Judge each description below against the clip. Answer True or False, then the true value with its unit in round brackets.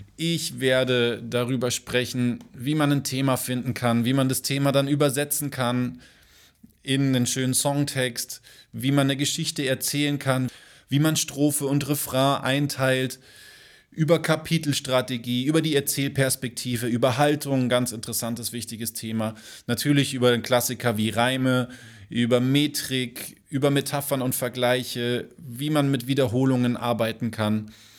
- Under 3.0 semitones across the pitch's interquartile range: True (2.5 semitones)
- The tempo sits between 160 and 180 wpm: False (135 wpm)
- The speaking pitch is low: True (130 Hz)